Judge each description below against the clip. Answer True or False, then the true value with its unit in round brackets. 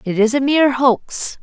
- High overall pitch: True (250 Hz)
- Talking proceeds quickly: True (210 wpm)